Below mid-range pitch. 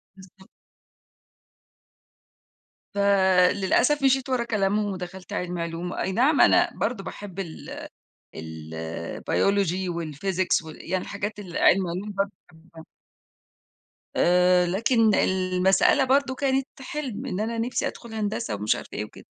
No: high, 190 Hz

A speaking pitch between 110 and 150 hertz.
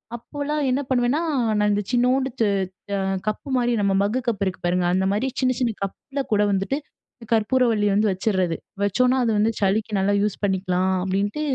No: high, 210 Hz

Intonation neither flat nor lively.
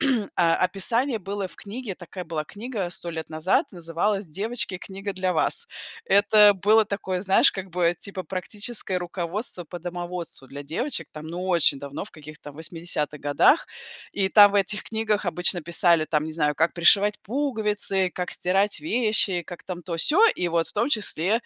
Yes: average, 3.6 semitones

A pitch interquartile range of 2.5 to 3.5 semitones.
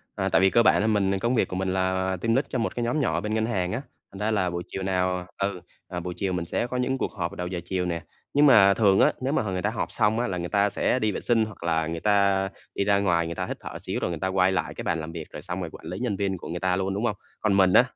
Yes: average, 3.1 semitones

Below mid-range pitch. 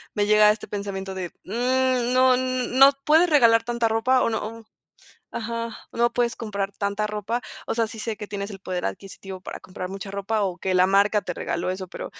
No: high, 215 Hz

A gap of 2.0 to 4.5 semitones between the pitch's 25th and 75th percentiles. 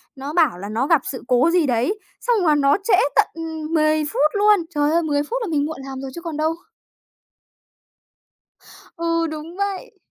Yes: average, 2.9 semitones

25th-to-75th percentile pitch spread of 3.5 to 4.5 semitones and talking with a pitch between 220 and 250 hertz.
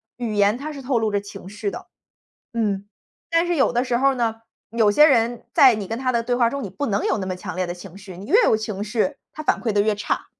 Yes: average, 3.9 semitones; high, 225 Hz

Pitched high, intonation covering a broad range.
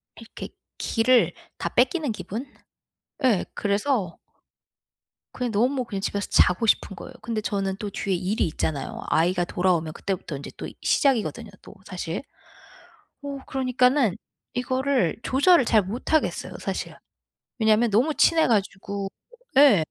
No: high, 215 Hz; average, 5.0 semitones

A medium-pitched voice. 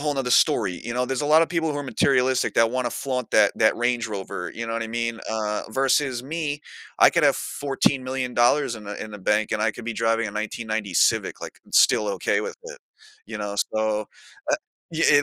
No: low, 120 Hz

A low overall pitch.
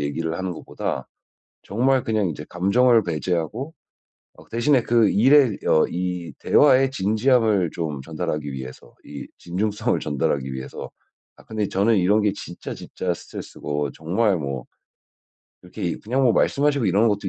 Yes: very low, 95 Hz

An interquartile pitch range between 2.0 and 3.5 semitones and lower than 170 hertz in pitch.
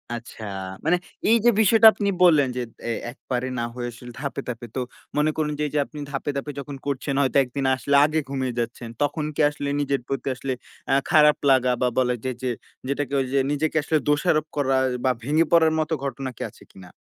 Yes: average, 2.7 semitones; medium, 140 Hz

